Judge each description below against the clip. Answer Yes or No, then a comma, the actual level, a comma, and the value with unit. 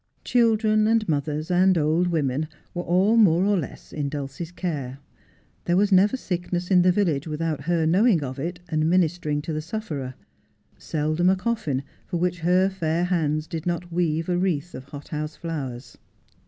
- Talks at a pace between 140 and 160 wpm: No, average, 175 wpm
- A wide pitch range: No, average, 3.2 semitones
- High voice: No, medium, 170 Hz